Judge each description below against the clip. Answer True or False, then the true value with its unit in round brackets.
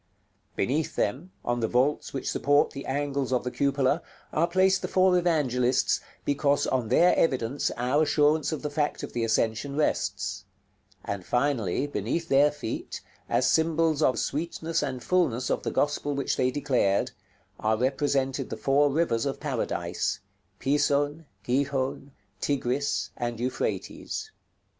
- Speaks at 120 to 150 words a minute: True (145 wpm)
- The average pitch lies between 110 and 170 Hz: True (140 Hz)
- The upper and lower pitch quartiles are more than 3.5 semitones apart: False (3.0 semitones)